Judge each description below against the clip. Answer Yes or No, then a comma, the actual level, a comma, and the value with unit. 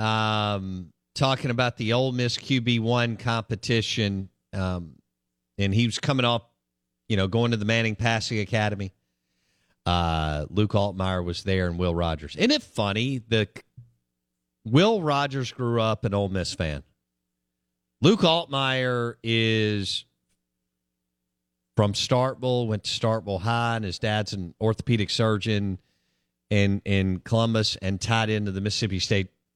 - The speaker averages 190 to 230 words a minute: No, slow, 135 wpm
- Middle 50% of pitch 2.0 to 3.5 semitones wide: No, average, 5.3 semitones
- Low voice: Yes, low, 105 Hz